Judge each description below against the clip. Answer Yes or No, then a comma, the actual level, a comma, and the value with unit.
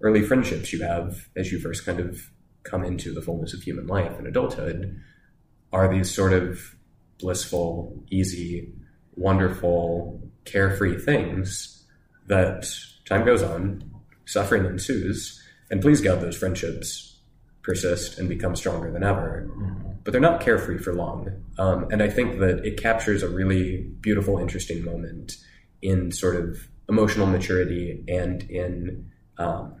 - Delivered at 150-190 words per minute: No, average, 140 wpm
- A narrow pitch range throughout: Yes, narrow, 1.9 semitones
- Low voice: Yes, very low, 90 Hz